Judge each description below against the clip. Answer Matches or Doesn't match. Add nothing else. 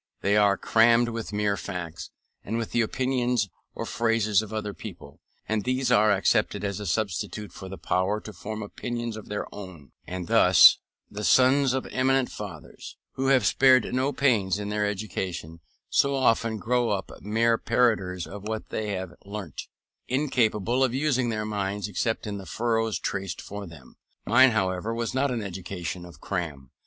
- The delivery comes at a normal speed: Matches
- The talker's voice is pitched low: Matches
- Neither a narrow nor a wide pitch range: Matches